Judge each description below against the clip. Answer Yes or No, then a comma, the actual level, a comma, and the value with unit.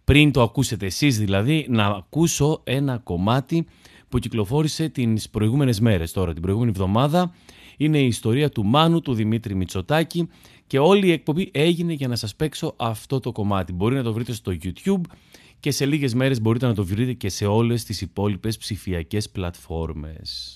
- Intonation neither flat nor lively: No, wide, 6.1 semitones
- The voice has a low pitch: Yes, low, 120 Hz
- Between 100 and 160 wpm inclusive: No, fast, 170 wpm